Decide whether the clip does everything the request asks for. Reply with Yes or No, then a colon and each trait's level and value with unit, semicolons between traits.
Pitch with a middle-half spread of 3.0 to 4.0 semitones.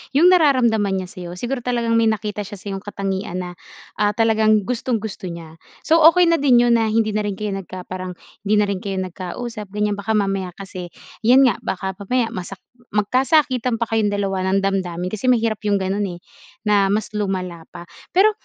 Yes: average, 3.3 semitones